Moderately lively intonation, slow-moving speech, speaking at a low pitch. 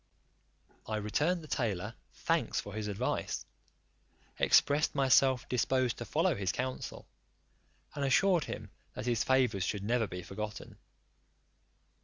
Yes: average, 4.2 semitones; slow, 125 wpm; low, 120 Hz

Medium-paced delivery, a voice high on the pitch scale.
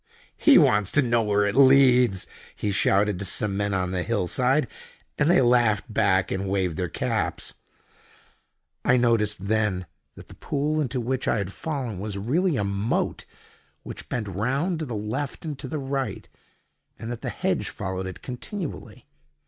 No: average, 175 wpm; low, 110 Hz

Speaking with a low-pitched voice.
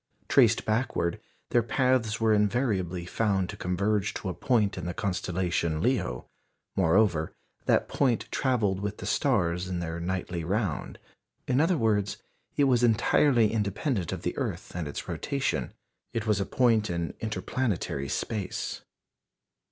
Yes: low, 105 Hz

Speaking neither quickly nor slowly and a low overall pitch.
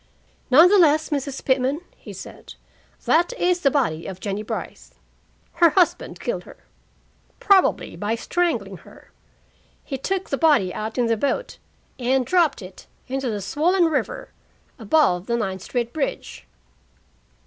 No: average, 145 wpm; very high, 270 Hz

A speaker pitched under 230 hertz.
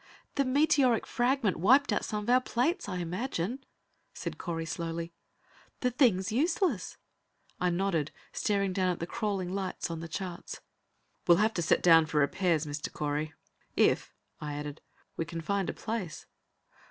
Yes: medium, 185 Hz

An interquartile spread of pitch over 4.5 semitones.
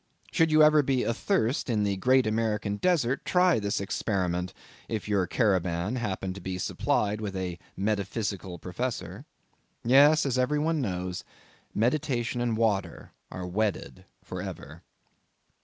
Yes: average, 5.2 semitones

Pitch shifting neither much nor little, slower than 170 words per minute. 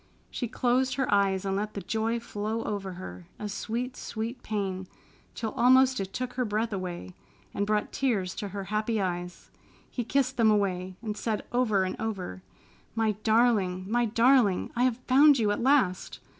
No: average, 3.8 semitones; average, 175 wpm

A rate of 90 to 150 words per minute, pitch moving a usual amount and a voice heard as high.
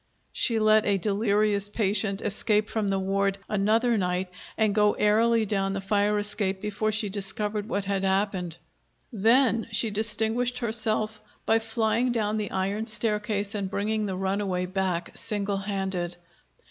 No: average, 145 wpm; narrow, 1.8 semitones; high, 210 Hz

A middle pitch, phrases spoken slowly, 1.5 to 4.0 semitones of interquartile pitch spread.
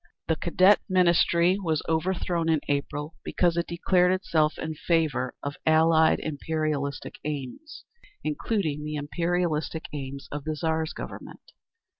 Yes: medium, 160 Hz; slow, 125 wpm; narrow, 2.4 semitones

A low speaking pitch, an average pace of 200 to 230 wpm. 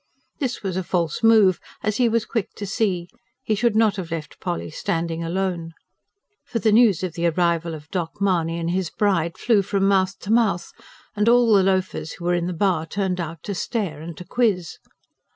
No: medium, 185 Hz; fast, 205 wpm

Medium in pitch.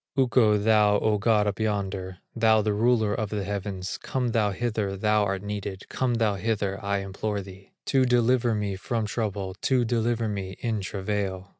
No: low, 105 Hz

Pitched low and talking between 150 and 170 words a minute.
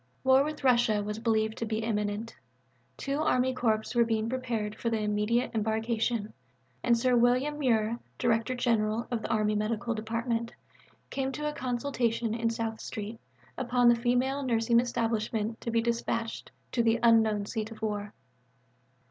No: high, 230 Hz; average, 155 wpm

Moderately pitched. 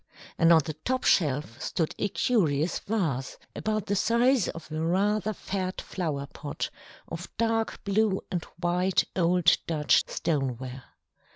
Yes: medium, 175 Hz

